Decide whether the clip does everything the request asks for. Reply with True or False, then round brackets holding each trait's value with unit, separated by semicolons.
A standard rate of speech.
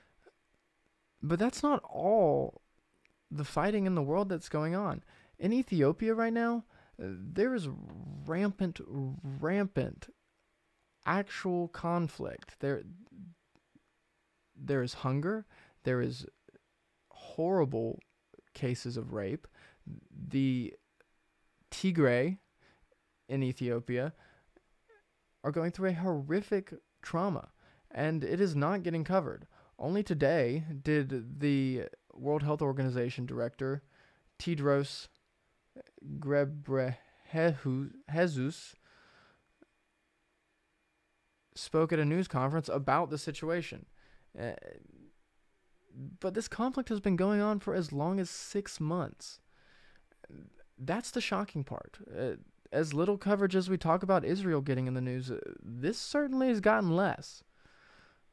False (105 wpm)